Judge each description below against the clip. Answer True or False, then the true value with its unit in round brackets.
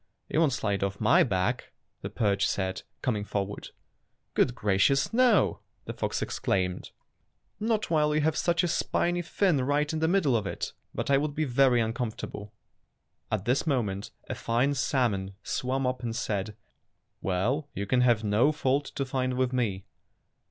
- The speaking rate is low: False (170 wpm)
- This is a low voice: True (125 Hz)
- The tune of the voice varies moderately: False (6.0 semitones)